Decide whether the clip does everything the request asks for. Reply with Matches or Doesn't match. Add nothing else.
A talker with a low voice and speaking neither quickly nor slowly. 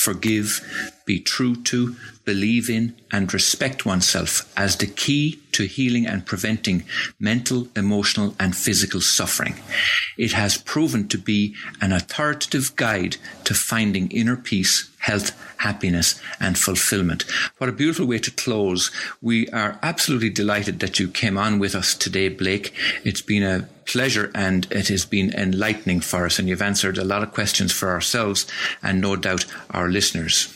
Matches